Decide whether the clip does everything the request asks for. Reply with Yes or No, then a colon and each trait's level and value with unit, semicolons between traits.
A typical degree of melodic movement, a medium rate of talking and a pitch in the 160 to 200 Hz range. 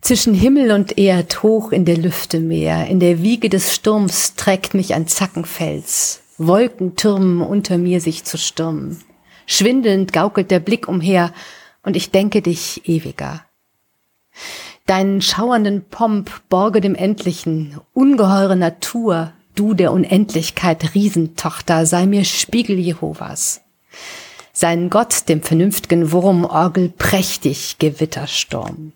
No: average, 3.2 semitones; slow, 120 wpm; medium, 185 Hz